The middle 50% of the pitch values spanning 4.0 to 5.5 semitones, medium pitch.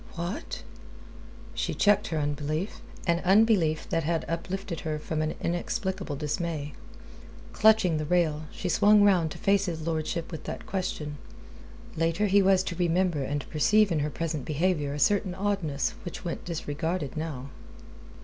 No: average, 3.6 semitones; medium, 165 Hz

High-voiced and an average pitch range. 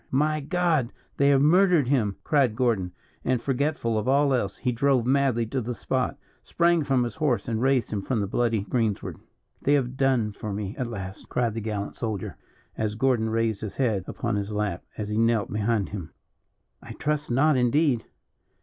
No: low, 120 Hz; average, 4.3 semitones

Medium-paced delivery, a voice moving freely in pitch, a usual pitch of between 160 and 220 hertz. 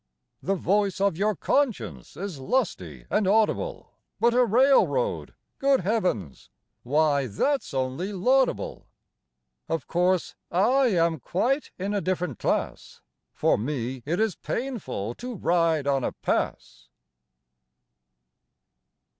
No: slow, 115 wpm; wide, 8.8 semitones; medium, 185 Hz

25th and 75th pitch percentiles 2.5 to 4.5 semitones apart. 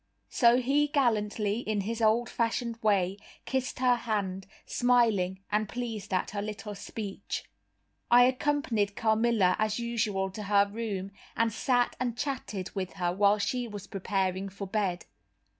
Yes: average, 3.1 semitones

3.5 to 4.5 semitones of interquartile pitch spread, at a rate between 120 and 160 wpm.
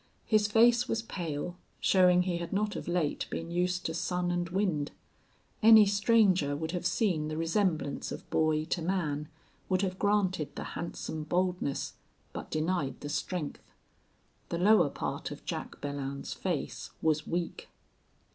Yes: average, 3.8 semitones; average, 150 wpm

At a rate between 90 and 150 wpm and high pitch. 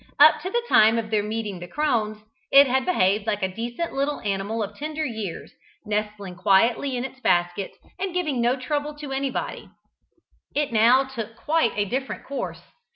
No: average, 175 wpm; high, 235 Hz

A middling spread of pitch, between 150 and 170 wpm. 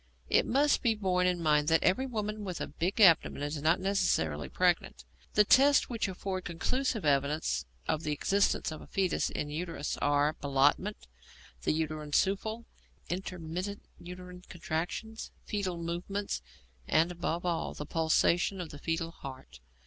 Yes: average, 4.2 semitones; average, 155 wpm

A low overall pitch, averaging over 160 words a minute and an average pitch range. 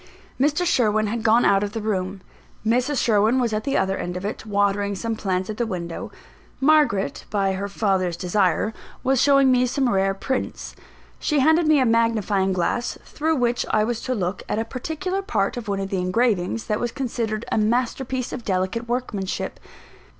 No: high, 220 Hz; average, 190 wpm; average, 4.3 semitones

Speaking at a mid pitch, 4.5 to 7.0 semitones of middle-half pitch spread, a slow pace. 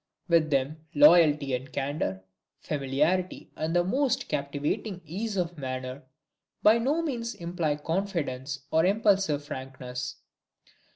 Yes: medium, 155 Hz; wide, 5.4 semitones; slow, 115 wpm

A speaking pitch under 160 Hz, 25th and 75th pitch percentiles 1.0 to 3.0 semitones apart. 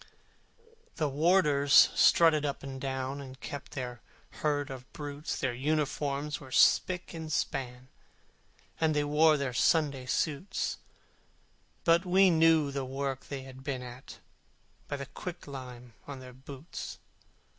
Yes: medium, 140 Hz; narrow, 2.6 semitones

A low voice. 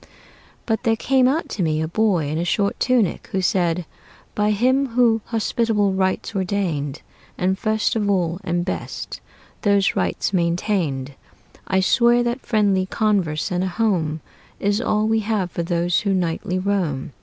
No: high, 195 Hz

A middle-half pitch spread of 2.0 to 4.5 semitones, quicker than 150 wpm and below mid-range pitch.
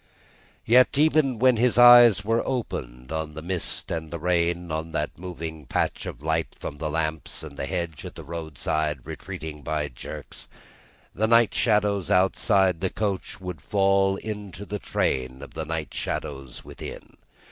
No: average, 4.9 semitones; average, 160 wpm; very low, 85 Hz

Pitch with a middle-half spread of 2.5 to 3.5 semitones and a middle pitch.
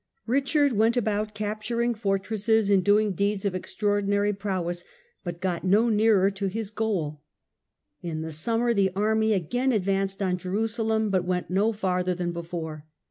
No: average, 3.1 semitones; high, 200 Hz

